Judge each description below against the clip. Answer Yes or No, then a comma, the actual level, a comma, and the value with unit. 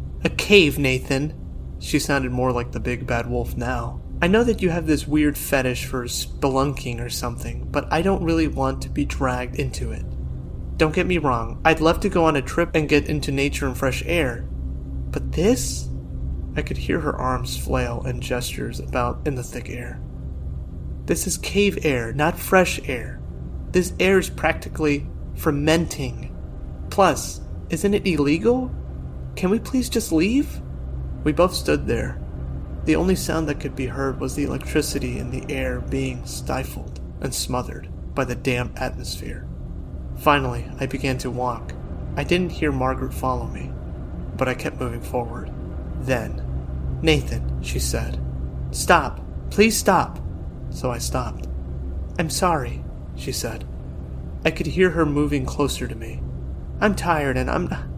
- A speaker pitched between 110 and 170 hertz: No, very low, 85 Hz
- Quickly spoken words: No, average, 160 wpm